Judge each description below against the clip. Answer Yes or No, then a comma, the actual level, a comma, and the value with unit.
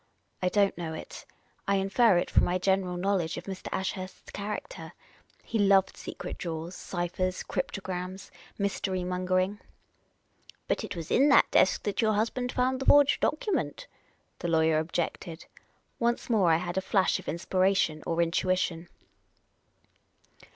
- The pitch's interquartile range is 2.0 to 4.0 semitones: Yes, narrow, 2.5 semitones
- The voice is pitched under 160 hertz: No, medium, 185 Hz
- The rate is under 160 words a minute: Yes, average, 150 wpm